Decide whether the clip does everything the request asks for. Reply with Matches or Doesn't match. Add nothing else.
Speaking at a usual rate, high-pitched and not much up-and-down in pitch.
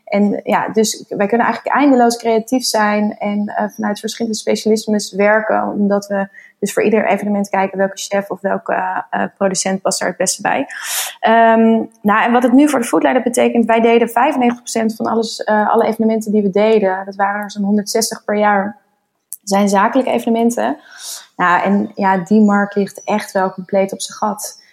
Matches